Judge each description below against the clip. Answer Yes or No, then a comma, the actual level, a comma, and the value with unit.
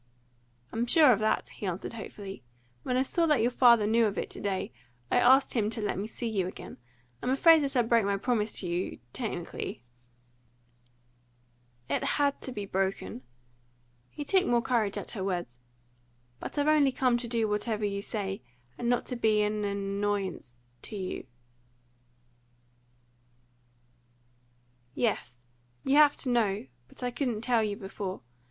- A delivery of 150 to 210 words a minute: Yes, average, 165 wpm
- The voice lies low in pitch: No, high, 210 Hz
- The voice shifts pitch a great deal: Yes, wide, 5.8 semitones